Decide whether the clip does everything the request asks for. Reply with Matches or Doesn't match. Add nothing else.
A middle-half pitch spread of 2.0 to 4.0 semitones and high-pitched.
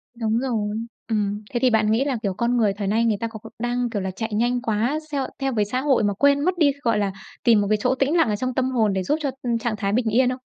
Matches